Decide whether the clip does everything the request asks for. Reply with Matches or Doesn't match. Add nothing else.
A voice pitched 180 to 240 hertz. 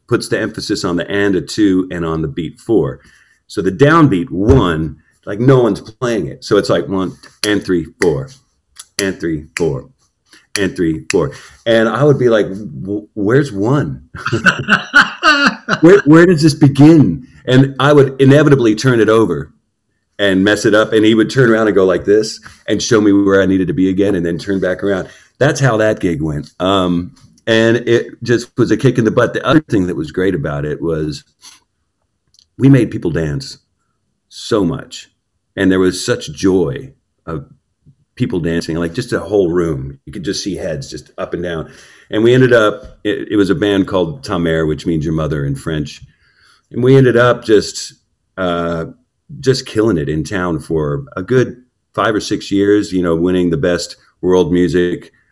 Doesn't match